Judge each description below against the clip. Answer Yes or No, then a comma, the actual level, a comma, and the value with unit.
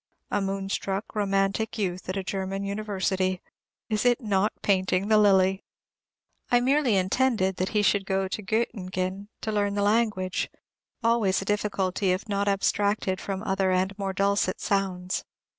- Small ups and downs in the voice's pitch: Yes, narrow, 1.7 semitones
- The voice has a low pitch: No, high, 195 Hz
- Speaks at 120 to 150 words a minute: Yes, average, 145 wpm